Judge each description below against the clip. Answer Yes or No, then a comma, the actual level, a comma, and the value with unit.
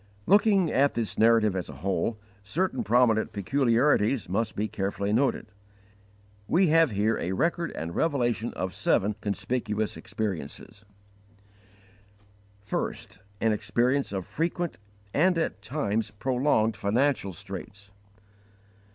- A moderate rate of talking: No, slow, 115 wpm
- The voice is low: Yes, low, 110 Hz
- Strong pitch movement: Yes, wide, 5.8 semitones